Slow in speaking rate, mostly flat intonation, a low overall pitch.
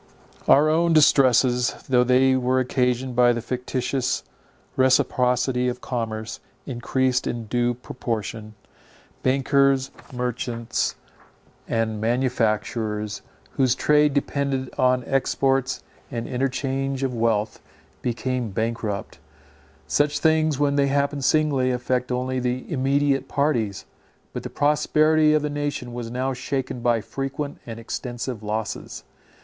Yes: slow, 115 wpm; narrow, 2.3 semitones; low, 130 Hz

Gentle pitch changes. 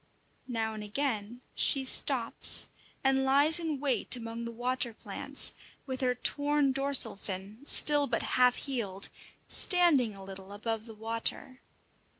No: average, 3.7 semitones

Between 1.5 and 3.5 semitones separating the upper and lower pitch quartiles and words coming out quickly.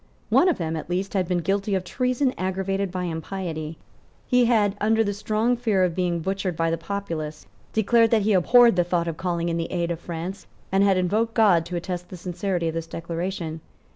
Yes: average, 3.2 semitones; fast, 210 wpm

